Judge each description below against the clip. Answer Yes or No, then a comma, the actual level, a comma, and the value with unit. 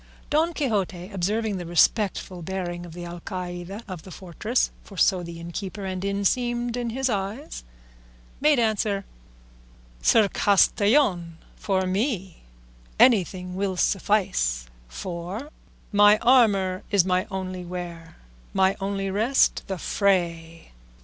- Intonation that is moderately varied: Yes, average, 3.3 semitones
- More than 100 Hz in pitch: Yes, high, 190 Hz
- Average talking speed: No, slow, 120 wpm